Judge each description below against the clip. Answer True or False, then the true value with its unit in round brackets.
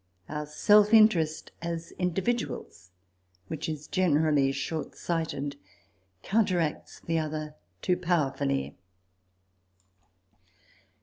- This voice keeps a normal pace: False (80 wpm)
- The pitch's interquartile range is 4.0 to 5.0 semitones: False (3.3 semitones)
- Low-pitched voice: False (160 Hz)